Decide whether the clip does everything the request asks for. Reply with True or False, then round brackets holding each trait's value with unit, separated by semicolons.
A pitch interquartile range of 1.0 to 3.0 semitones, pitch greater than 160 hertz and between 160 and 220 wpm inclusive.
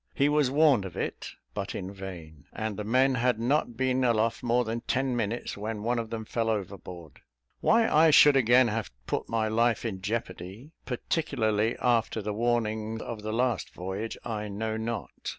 False (2.7 semitones; 115 Hz; 180 wpm)